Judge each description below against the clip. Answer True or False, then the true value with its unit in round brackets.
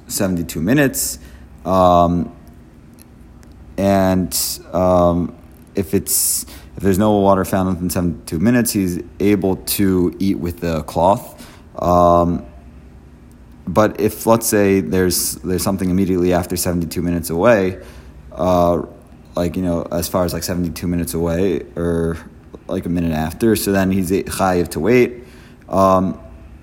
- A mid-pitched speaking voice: False (90 Hz)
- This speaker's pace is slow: True (130 wpm)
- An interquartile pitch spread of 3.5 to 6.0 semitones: False (2.7 semitones)